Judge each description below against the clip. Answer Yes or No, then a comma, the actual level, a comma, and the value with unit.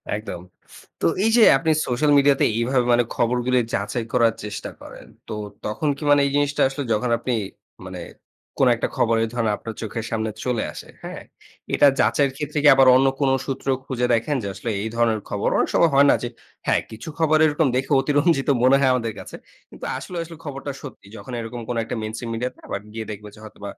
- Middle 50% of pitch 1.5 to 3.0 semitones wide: No, average, 4.0 semitones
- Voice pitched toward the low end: Yes, low, 125 Hz